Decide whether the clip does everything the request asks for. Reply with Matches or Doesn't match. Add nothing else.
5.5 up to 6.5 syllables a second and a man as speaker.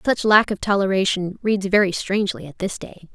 Doesn't match